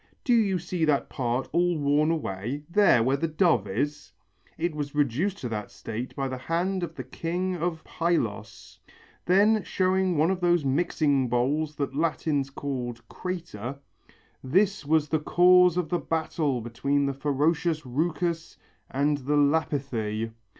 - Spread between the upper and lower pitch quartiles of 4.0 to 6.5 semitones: Yes, average, 4.6 semitones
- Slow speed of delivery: No, average, 150 wpm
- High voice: No, medium, 150 Hz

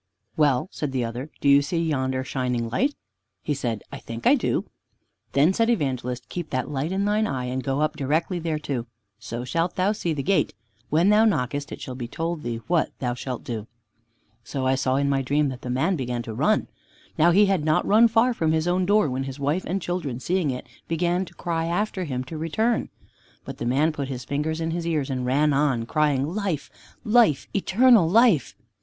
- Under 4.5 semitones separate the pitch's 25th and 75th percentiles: No, average, 5.3 semitones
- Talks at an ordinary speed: No, fast, 210 wpm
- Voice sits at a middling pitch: Yes, medium, 150 Hz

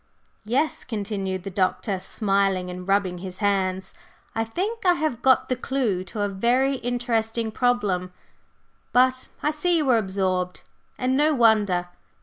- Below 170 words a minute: Yes, average, 145 wpm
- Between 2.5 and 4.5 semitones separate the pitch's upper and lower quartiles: No, average, 5.1 semitones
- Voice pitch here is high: Yes, high, 220 Hz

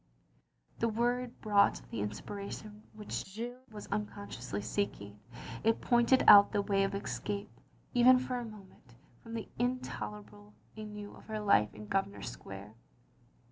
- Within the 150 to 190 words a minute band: No, average, 140 wpm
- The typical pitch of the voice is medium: No, high, 205 Hz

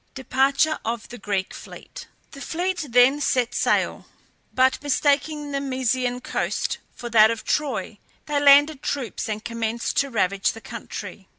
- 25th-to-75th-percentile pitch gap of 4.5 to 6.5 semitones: No, average, 3.7 semitones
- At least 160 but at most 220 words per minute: No, average, 150 wpm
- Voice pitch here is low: No, very high, 260 Hz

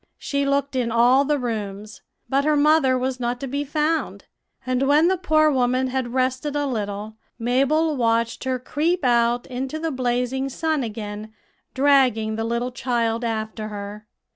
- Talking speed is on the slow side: No, average, 165 wpm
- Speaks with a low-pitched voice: No, very high, 255 Hz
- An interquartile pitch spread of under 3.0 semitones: No, average, 3.4 semitones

